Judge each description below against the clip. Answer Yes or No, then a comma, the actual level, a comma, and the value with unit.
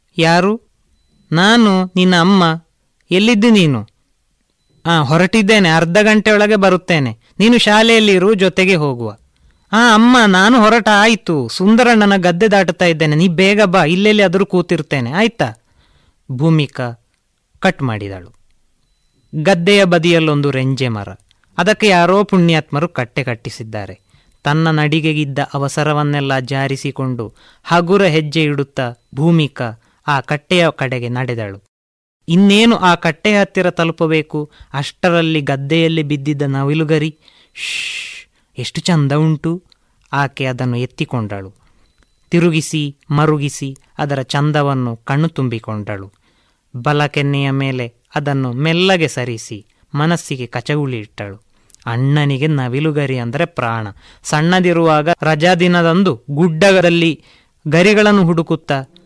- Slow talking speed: No, average, 95 wpm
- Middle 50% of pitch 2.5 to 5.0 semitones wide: No, wide, 5.5 semitones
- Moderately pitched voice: Yes, medium, 150 Hz